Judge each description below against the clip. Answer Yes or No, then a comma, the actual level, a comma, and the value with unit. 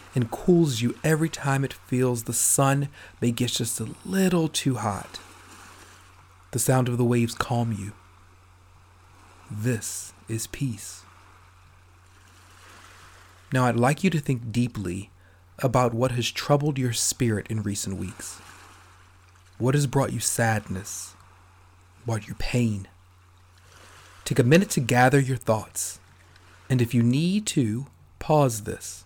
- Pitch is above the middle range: No, low, 105 Hz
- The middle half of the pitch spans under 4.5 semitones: No, wide, 5.5 semitones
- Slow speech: Yes, slow, 130 wpm